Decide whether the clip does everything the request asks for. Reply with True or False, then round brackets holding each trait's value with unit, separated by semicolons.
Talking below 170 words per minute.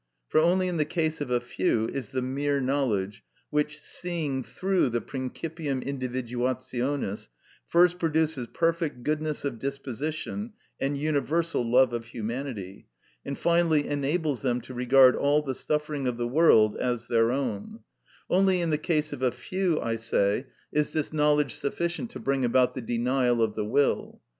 True (160 wpm)